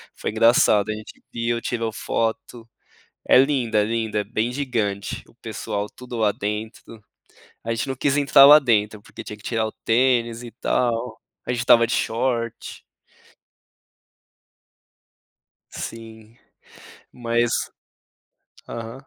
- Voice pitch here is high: No, low, 115 Hz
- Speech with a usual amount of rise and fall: No, narrow, 1.9 semitones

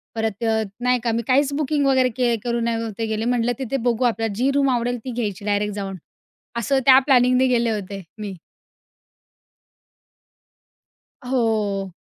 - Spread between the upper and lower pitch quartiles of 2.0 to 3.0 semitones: Yes, average, 2.7 semitones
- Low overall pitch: No, high, 235 Hz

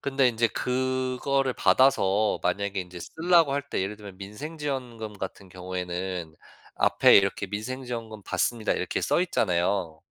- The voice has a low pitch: Yes, low, 110 Hz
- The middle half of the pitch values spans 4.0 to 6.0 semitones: Yes, wide, 5.4 semitones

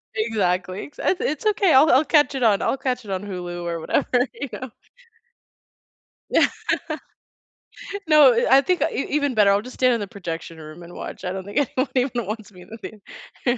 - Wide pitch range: Yes, wide, 6.2 semitones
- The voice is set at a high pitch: Yes, high, 225 Hz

